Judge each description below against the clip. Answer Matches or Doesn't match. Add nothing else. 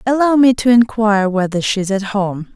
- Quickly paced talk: Matches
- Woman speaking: Matches